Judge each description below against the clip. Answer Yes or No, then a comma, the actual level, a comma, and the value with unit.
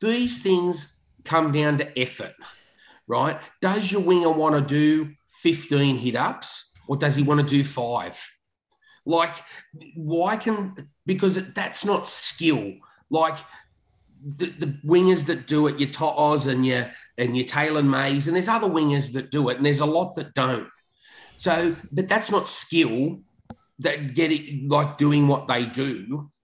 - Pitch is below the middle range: No, medium, 150 Hz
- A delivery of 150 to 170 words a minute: Yes, average, 165 wpm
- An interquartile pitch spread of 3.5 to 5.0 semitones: Yes, average, 3.8 semitones